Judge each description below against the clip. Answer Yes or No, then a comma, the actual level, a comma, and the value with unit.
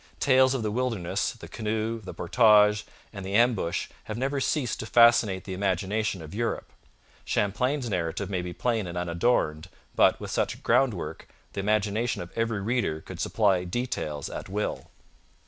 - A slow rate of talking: No, average, 165 wpm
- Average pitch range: Yes, average, 4.2 semitones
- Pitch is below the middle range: Yes, low, 105 Hz